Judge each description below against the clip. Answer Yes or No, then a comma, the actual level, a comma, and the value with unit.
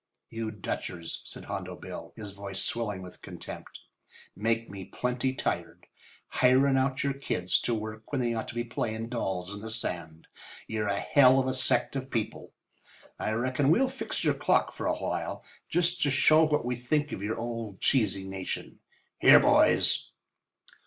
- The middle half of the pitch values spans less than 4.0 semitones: No, average, 4.4 semitones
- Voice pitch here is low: Yes, low, 115 Hz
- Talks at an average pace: Yes, average, 175 wpm